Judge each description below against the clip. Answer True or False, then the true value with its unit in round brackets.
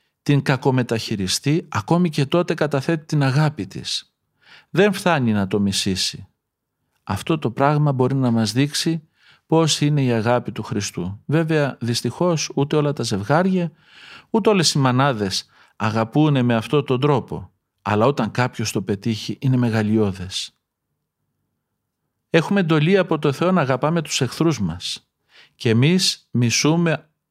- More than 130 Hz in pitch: True (140 Hz)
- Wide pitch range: True (5.8 semitones)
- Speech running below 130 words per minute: False (135 wpm)